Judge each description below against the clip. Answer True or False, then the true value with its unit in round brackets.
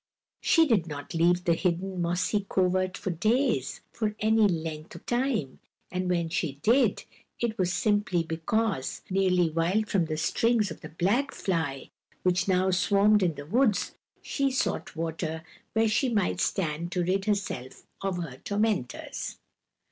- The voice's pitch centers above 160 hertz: True (185 Hz)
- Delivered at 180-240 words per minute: False (155 wpm)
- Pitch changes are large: False (4.3 semitones)